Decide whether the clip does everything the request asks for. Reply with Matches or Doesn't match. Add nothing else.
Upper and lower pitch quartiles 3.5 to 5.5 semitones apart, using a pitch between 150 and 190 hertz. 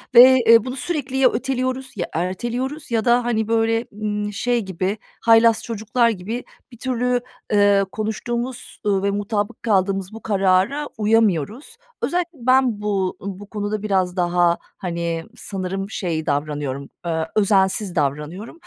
Doesn't match